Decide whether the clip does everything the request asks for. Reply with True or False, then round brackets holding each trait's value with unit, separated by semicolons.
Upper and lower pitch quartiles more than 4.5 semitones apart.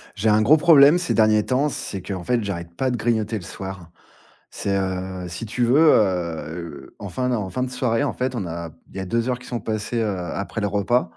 True (5.0 semitones)